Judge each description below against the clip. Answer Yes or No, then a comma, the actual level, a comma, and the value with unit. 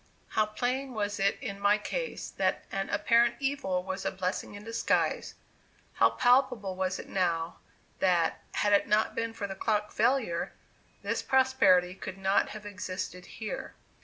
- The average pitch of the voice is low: No, high, 205 Hz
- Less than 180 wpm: Yes, average, 160 wpm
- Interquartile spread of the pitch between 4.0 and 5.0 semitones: No, average, 3.5 semitones